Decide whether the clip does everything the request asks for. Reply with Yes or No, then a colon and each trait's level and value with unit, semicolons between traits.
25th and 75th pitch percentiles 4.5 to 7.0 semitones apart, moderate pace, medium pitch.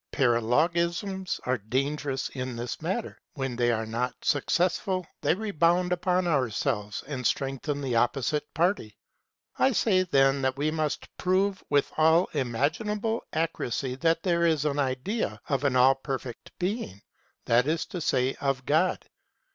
Yes: average, 5.3 semitones; average, 145 wpm; medium, 145 Hz